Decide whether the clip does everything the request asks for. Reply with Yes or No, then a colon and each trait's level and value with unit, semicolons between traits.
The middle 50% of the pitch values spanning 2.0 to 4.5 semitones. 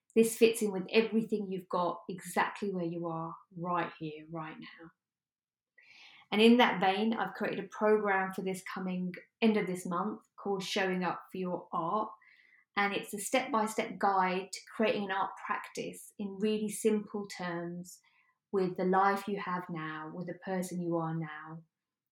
Yes: average, 3.4 semitones